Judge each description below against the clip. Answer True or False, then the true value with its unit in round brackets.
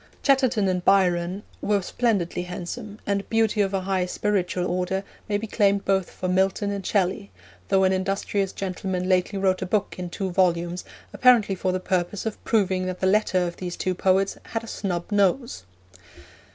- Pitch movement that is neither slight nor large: False (2.0 semitones)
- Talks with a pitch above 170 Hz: True (190 Hz)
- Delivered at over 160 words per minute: True (180 wpm)